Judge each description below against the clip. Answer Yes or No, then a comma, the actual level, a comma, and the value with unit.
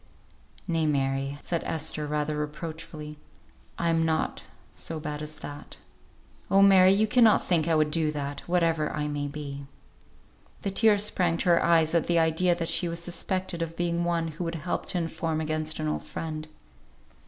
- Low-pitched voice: No, medium, 160 Hz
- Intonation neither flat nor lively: No, narrow, 2.1 semitones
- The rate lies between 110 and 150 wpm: No, average, 175 wpm